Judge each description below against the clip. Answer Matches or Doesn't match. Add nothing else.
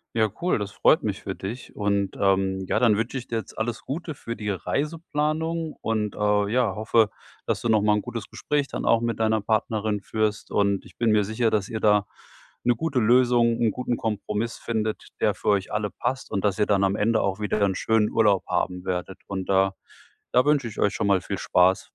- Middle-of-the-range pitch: Doesn't match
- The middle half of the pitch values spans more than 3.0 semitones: Doesn't match